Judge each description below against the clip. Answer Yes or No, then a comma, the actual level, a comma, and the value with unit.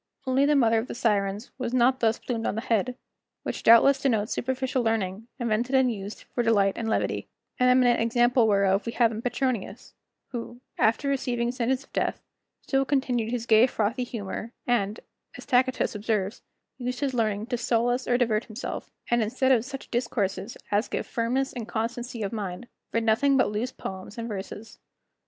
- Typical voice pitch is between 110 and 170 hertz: No, high, 235 Hz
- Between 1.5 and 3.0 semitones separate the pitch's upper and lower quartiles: Yes, narrow, 2.6 semitones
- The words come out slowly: No, average, 180 wpm